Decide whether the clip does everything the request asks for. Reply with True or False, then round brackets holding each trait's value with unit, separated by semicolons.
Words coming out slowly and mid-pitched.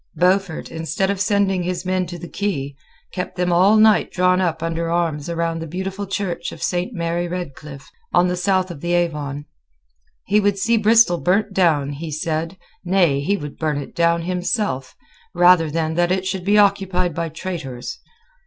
False (180 wpm; 175 Hz)